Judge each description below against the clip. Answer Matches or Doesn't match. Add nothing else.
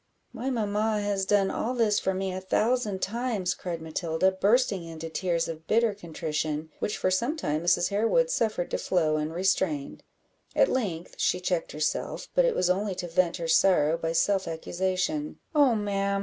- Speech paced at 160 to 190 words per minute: Matches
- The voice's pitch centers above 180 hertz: Matches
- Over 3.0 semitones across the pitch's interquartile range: Matches